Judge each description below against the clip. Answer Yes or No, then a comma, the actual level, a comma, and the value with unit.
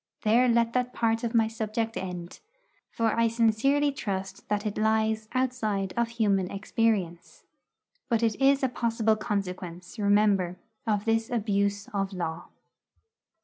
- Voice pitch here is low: No, high, 220 Hz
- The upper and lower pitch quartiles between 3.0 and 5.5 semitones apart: No, narrow, 2.6 semitones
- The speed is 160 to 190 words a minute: No, average, 140 wpm